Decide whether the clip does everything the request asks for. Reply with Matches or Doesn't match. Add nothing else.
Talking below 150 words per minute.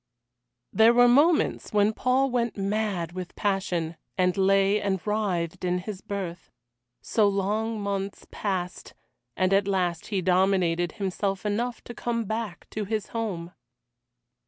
Matches